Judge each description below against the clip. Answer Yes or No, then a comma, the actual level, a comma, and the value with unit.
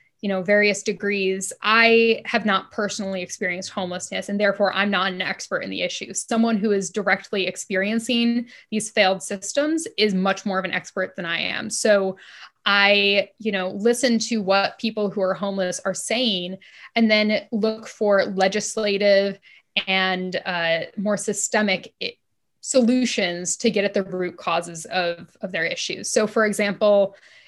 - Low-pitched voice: No, high, 200 Hz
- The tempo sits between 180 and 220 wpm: No, average, 155 wpm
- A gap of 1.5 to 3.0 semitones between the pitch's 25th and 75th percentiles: Yes, narrow, 2.4 semitones